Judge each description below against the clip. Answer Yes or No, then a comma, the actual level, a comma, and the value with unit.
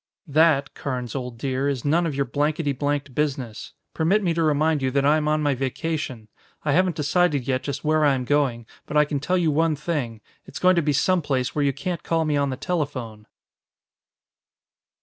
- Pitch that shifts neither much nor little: Yes, average, 3.0 semitones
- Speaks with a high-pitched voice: No, medium, 145 Hz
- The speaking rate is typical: No, fast, 210 wpm